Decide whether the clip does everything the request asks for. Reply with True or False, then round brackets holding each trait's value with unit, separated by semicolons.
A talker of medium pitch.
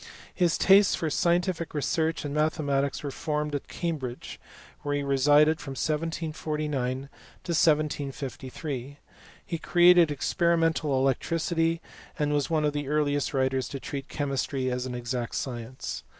True (150 Hz)